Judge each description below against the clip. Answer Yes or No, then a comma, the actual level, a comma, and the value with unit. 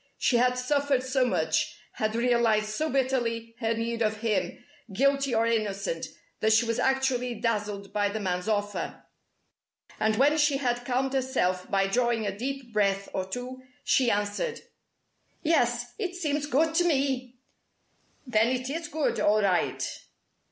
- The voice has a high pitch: Yes, high, 240 Hz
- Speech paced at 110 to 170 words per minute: Yes, average, 150 wpm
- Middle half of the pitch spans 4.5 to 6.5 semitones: No, average, 3.9 semitones